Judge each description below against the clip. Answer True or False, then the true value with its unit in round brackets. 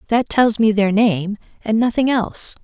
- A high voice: True (220 Hz)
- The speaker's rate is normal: True (180 wpm)